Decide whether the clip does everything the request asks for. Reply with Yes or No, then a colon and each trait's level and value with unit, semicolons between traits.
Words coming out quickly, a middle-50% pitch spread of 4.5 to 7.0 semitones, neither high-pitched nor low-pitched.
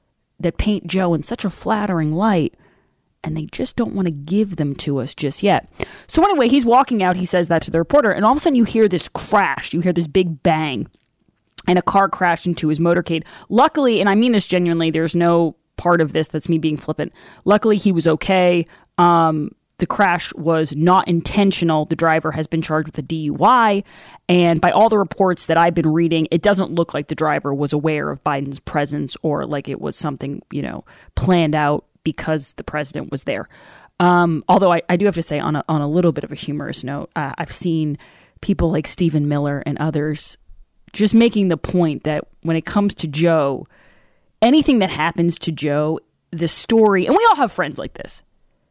No: fast, 210 wpm; average, 3.8 semitones; medium, 170 Hz